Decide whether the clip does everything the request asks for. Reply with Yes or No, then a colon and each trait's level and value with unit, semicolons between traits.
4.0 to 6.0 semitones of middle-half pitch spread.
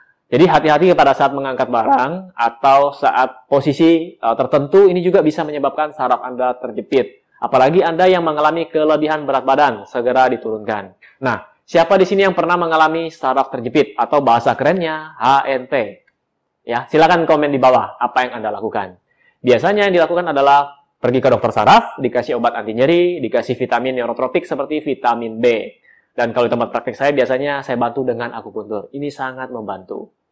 Yes: average, 4.3 semitones